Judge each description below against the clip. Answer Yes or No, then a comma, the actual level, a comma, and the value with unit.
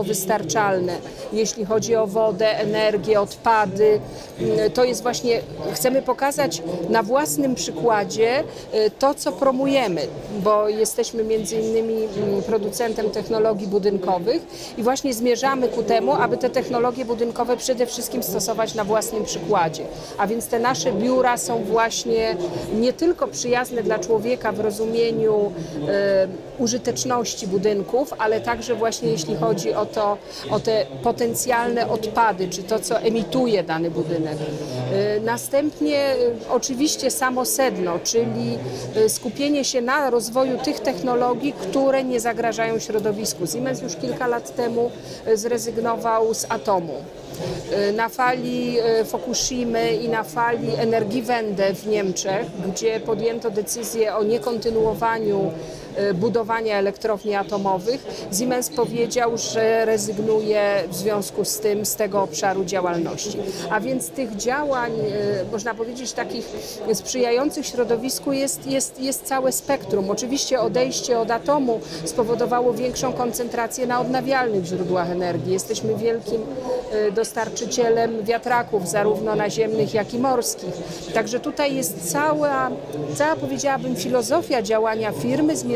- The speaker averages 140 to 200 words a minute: No, average, 120 wpm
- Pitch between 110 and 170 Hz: No, high, 225 Hz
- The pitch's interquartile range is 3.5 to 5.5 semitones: No, average, 2.8 semitones